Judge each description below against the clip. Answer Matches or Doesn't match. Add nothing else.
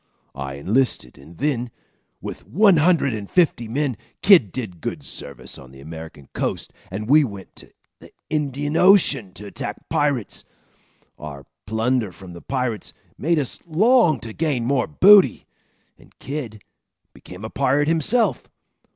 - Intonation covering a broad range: Matches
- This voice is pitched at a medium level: Doesn't match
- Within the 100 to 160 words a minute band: Matches